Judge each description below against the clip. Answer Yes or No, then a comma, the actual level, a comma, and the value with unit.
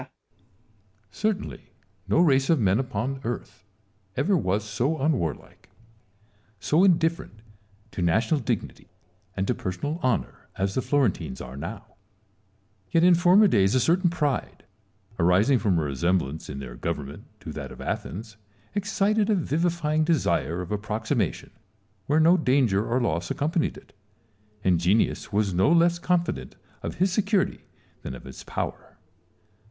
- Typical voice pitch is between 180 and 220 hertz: No, low, 125 Hz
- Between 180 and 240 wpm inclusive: No, average, 145 wpm